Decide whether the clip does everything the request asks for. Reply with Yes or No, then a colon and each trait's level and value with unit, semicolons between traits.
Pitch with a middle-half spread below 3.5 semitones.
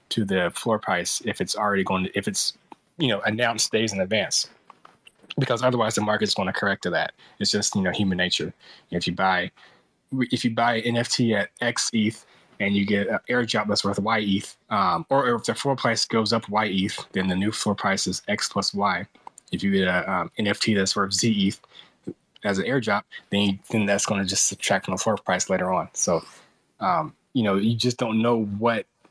Yes: average, 2.9 semitones